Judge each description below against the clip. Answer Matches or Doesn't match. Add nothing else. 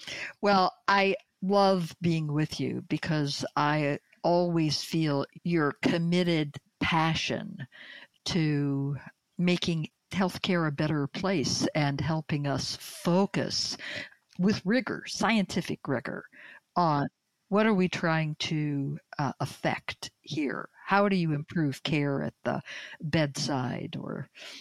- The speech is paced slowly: Matches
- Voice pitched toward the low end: Doesn't match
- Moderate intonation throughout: Matches